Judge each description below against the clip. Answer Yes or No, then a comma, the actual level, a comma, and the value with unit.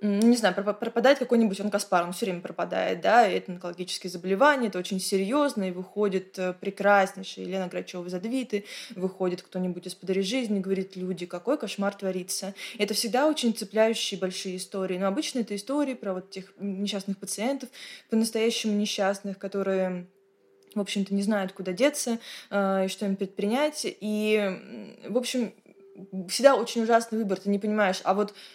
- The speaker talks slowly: No, fast, 160 wpm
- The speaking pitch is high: Yes, high, 200 Hz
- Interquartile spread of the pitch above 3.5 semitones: No, average, 3.0 semitones